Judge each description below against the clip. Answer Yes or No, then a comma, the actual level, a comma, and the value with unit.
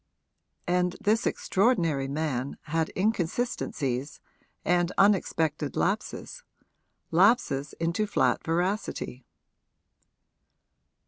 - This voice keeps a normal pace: No, slow, 70 wpm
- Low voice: No, medium, 175 Hz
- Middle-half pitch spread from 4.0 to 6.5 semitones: Yes, average, 5.1 semitones